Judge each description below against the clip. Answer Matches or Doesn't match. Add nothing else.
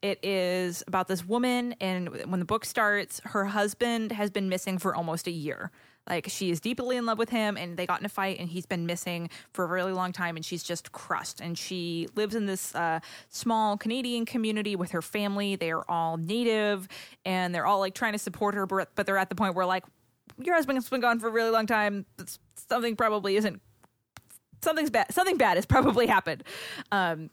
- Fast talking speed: Matches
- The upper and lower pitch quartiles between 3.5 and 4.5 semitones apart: Matches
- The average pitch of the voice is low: Doesn't match